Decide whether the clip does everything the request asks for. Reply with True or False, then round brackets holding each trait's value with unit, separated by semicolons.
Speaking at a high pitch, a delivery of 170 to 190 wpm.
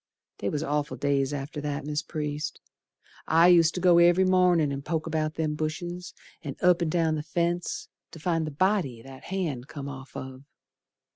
False (155 Hz; 185 wpm)